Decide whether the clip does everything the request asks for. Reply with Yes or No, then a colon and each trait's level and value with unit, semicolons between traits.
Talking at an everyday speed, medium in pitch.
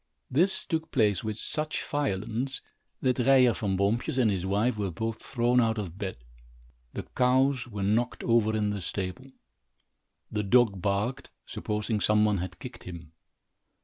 No: average, 155 wpm; low, 110 Hz